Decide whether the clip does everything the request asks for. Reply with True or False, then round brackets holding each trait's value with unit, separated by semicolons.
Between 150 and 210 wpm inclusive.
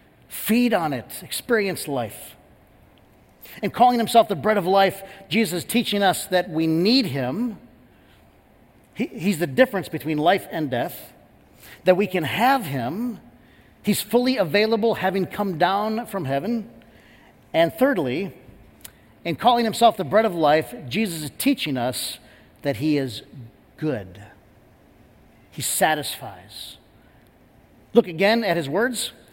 False (135 wpm)